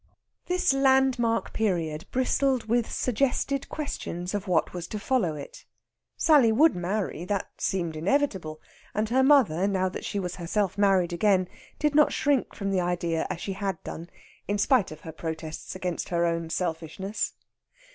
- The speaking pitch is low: No, high, 195 Hz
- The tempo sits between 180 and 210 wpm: No, average, 160 wpm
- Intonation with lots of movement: Yes, wide, 6.2 semitones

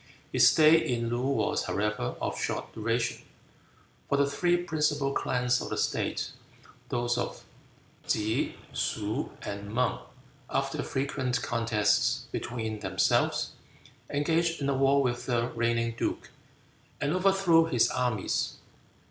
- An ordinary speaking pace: No, slow, 125 wpm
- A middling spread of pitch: Yes, average, 3.7 semitones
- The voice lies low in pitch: Yes, low, 125 Hz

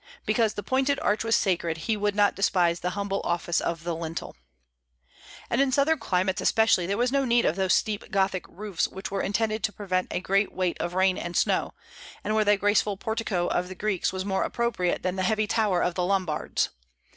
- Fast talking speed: Yes, fast, 210 wpm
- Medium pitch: No, high, 195 Hz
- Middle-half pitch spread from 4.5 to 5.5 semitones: No, average, 3.0 semitones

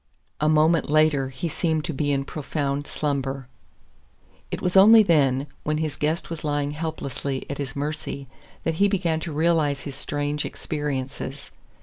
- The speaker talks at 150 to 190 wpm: Yes, average, 160 wpm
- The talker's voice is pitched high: No, medium, 150 Hz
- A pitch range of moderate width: No, narrow, 2.2 semitones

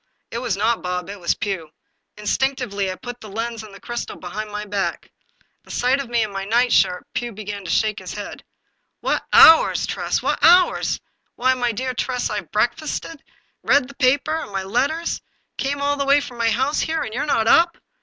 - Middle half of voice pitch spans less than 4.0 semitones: No, average, 4.8 semitones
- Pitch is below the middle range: No, high, 235 Hz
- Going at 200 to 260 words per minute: Yes, fast, 205 wpm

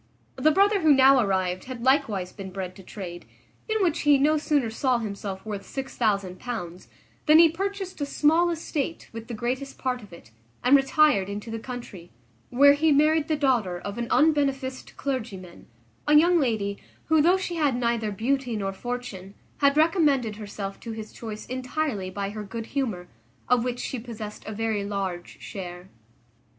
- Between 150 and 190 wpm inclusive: Yes, average, 170 wpm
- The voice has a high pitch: Yes, high, 245 Hz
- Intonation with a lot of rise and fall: Yes, wide, 6.2 semitones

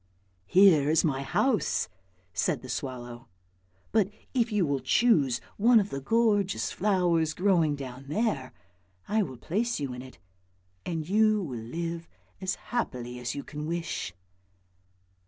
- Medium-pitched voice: Yes, medium, 160 Hz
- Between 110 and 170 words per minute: Yes, average, 150 wpm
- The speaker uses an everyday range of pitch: No, wide, 7.7 semitones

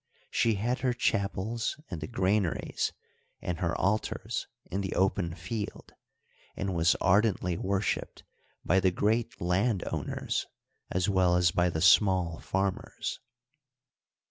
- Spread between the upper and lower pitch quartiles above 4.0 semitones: No, average, 2.8 semitones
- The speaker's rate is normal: No, slow, 125 wpm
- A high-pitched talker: No, very low, 95 Hz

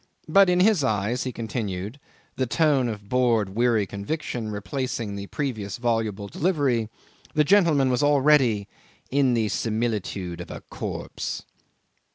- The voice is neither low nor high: No, low, 120 Hz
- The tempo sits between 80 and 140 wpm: Yes, slow, 135 wpm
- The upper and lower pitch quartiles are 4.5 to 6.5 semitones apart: Yes, average, 5.2 semitones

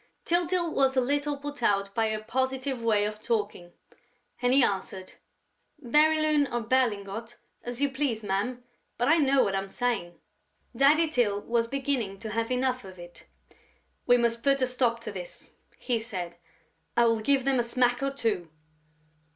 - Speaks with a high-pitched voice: Yes, high, 245 Hz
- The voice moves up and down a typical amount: Yes, average, 4.2 semitones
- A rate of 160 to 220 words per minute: Yes, average, 165 wpm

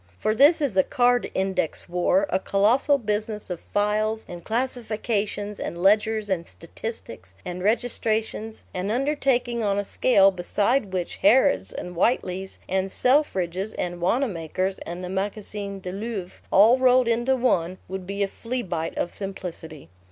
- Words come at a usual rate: Yes, average, 145 wpm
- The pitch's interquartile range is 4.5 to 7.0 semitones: No, average, 4.1 semitones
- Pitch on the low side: No, high, 205 Hz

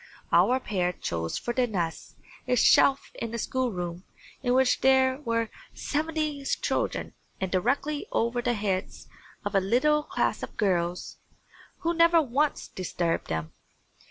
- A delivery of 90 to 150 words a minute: Yes, average, 140 wpm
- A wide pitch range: Yes, wide, 6.7 semitones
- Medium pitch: No, high, 240 Hz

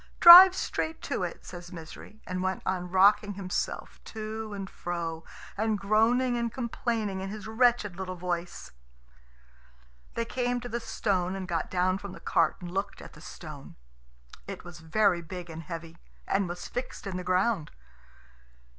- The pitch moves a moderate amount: Yes, average, 3.8 semitones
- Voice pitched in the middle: No, high, 195 Hz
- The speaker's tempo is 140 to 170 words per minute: Yes, average, 165 wpm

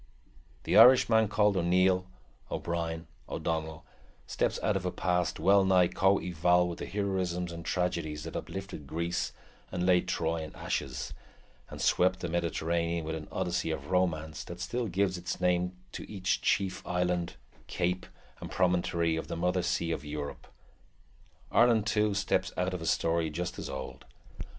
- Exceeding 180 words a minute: No, average, 160 wpm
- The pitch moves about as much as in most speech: No, narrow, 2.1 semitones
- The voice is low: Yes, very low, 90 Hz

